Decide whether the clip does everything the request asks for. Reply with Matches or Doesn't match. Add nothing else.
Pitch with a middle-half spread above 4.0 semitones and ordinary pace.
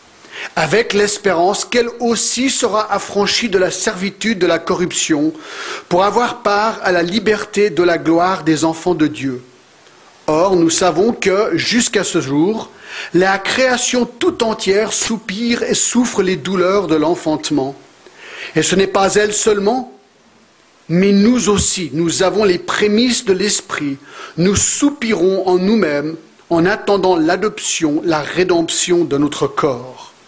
Doesn't match